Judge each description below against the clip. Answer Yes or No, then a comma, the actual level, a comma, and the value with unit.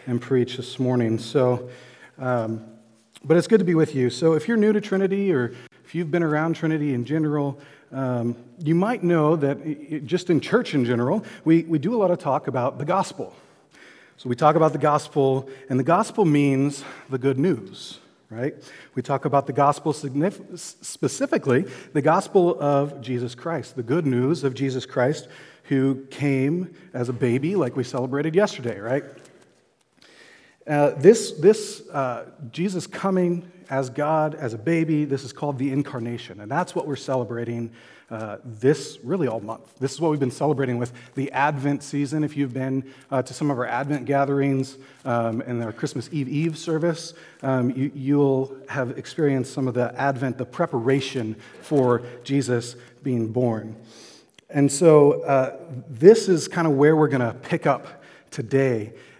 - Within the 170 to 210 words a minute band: Yes, average, 175 wpm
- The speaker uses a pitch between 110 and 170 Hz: Yes, medium, 140 Hz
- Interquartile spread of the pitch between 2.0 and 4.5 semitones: Yes, average, 3.8 semitones